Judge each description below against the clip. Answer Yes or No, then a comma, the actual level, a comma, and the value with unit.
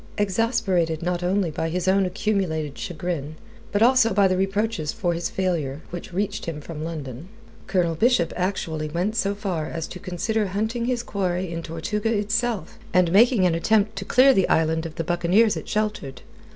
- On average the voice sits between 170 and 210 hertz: Yes, medium, 185 Hz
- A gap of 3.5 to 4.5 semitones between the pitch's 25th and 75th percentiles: Yes, average, 4.1 semitones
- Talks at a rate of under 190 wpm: Yes, average, 180 wpm